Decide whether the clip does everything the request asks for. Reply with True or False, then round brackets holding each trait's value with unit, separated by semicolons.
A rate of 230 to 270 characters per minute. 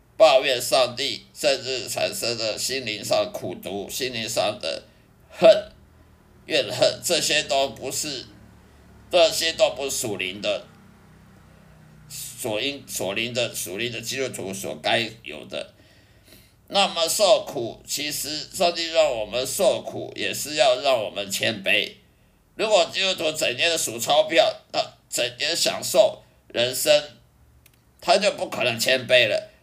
False (195 characters per minute)